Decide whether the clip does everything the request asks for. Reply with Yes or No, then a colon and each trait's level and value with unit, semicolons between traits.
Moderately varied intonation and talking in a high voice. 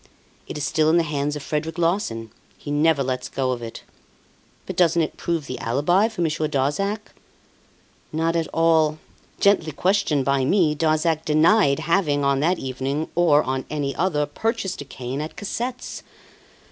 No: average, 3.4 semitones; medium, 155 Hz